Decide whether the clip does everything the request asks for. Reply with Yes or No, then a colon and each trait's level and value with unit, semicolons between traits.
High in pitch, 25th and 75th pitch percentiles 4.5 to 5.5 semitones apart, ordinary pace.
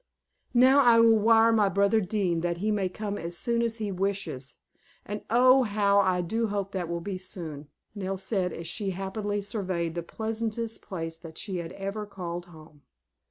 No: high, 200 Hz; average, 3.8 semitones; average, 185 wpm